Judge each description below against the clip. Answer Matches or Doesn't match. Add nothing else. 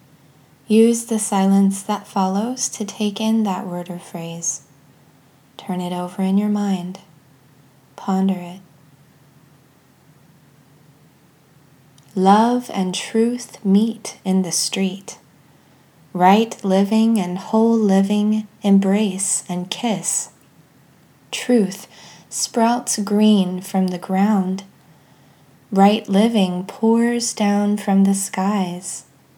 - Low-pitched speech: Doesn't match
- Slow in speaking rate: Matches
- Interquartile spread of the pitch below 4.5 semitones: Doesn't match